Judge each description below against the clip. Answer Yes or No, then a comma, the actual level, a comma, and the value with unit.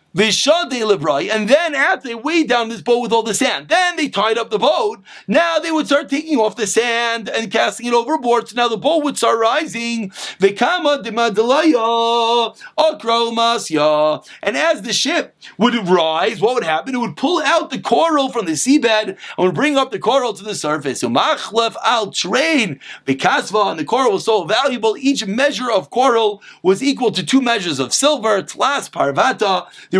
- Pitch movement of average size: Yes, average, 4.9 semitones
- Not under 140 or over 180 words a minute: Yes, average, 170 wpm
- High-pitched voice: Yes, high, 235 Hz